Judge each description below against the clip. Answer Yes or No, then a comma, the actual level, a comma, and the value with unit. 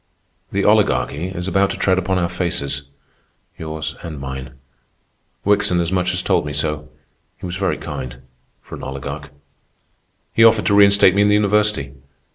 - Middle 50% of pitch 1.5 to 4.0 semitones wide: No, wide, 5.5 semitones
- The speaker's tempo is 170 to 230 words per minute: No, average, 155 wpm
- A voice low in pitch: Yes, very low, 90 Hz